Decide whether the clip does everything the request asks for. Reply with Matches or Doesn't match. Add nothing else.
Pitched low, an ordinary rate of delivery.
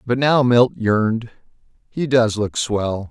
Matches